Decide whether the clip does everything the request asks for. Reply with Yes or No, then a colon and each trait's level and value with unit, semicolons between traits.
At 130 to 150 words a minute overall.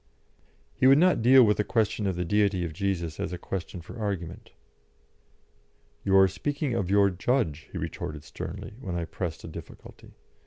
No: average, 180 wpm